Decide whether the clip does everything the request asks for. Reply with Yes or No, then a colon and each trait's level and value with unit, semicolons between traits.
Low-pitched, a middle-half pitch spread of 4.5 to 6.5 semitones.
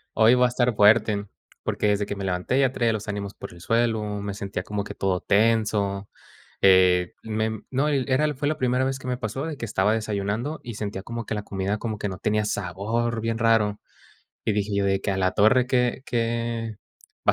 No: low, 110 Hz; average, 2.8 semitones